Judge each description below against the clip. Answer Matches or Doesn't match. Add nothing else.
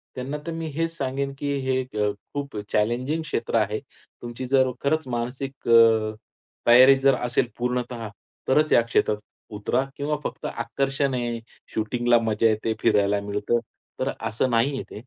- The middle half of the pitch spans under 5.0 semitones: Matches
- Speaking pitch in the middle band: Doesn't match